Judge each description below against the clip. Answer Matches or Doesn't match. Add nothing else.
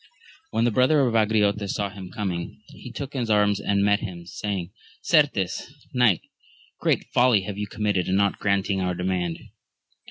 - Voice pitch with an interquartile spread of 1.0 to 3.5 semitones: Matches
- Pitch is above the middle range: Doesn't match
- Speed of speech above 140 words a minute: Matches